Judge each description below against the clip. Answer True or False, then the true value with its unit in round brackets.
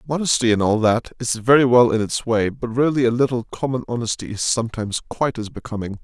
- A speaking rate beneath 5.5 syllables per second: False (6.3 syllables/s)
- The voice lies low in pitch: True (120 Hz)